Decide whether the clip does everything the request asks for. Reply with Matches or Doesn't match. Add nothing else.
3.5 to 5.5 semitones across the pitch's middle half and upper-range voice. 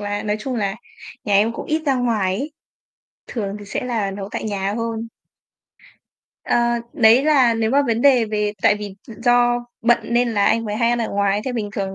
Doesn't match